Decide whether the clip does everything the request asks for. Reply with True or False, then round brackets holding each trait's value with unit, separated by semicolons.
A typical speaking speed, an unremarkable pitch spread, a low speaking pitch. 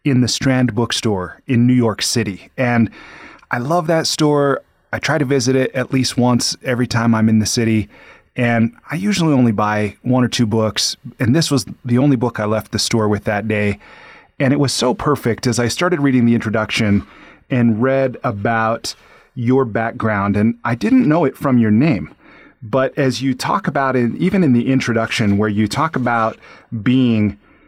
True (190 wpm; 3.2 semitones; 120 Hz)